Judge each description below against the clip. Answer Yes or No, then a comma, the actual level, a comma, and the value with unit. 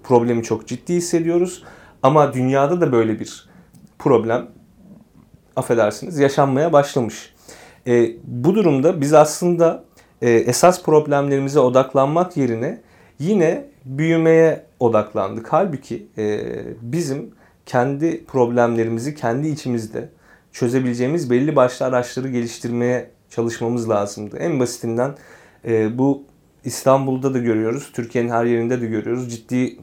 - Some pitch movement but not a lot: Yes, average, 3.7 semitones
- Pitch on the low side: Yes, low, 125 Hz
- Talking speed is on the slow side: No, average, 105 wpm